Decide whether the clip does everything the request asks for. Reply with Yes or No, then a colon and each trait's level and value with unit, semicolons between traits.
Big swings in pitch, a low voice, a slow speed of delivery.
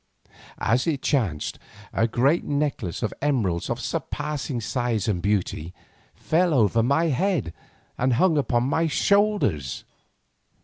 Yes: wide, 6.2 semitones; low, 125 Hz; slow, 125 wpm